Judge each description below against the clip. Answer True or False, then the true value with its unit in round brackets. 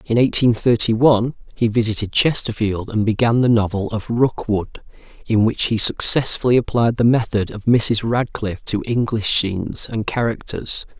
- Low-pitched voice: True (115 Hz)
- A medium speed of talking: True (155 wpm)